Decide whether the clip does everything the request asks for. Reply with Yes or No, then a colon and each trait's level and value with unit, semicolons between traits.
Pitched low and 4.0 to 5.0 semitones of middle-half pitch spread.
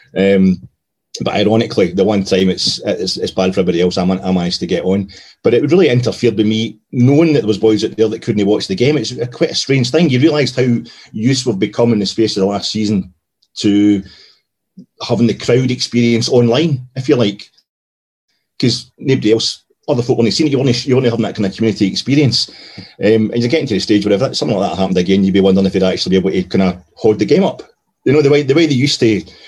Yes: low, 110 Hz; average, 4.6 semitones